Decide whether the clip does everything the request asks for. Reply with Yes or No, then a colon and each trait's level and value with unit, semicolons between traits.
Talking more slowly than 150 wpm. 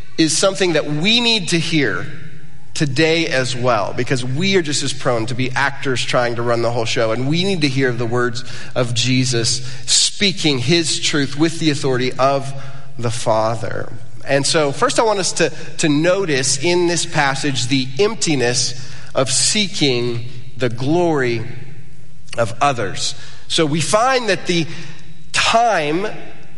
No: average, 155 wpm